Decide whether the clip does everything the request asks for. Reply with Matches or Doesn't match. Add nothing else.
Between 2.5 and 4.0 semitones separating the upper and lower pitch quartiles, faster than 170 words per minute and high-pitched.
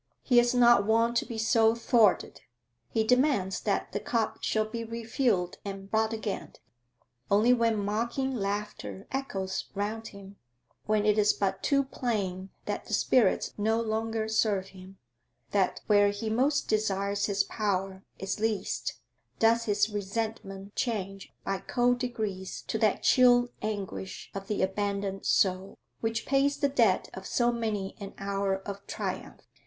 Doesn't match